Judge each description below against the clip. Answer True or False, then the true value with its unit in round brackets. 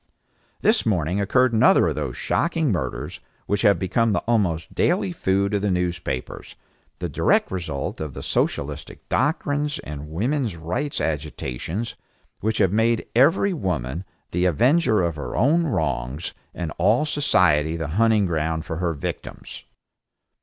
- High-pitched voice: False (95 Hz)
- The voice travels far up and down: True (6.8 semitones)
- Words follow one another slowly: False (145 wpm)